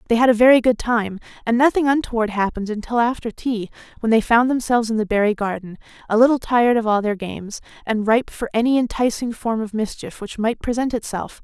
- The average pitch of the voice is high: Yes, high, 230 Hz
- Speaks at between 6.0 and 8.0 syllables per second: Yes, 6.1 syllables/s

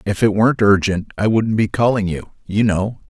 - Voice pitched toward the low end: Yes, low, 105 Hz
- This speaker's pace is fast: Yes, fast, 210 wpm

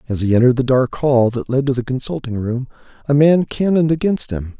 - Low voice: Yes, low, 130 Hz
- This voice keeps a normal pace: No, fast, 220 wpm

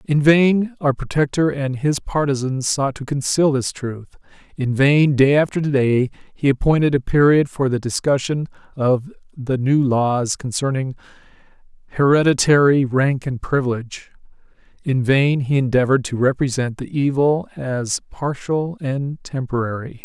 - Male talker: Yes, male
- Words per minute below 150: Yes, slow, 135 wpm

